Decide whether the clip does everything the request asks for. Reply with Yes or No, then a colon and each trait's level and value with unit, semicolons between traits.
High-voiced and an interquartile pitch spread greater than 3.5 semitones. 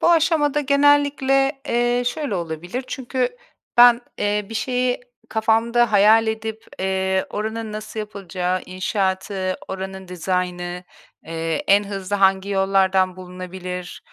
Yes: high, 205 Hz; average, 4.5 semitones